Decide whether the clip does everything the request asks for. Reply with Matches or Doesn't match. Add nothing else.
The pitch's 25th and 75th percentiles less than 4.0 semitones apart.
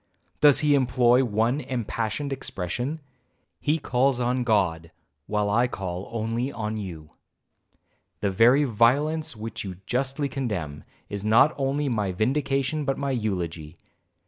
Doesn't match